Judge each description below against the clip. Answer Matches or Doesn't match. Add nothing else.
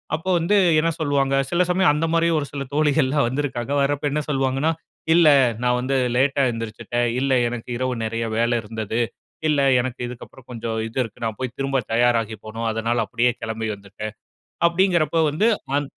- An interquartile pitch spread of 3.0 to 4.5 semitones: Matches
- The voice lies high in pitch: Doesn't match